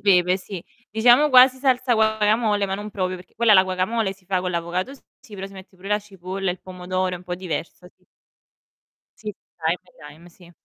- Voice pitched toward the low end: No, high, 190 Hz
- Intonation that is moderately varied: Yes, average, 3.1 semitones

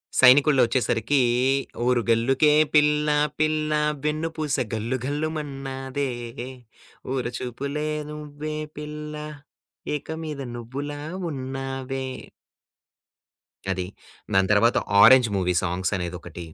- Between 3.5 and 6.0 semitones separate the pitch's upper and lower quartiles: Yes, average, 4.0 semitones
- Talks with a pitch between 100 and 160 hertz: Yes, low, 135 Hz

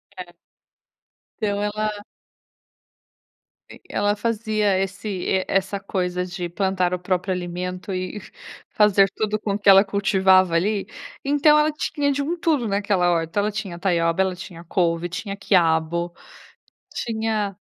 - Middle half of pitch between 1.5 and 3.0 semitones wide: Yes, average, 2.7 semitones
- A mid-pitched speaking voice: No, high, 195 Hz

